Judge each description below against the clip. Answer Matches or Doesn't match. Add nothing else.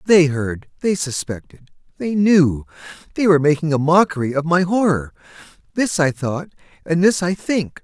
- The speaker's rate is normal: Doesn't match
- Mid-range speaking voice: Matches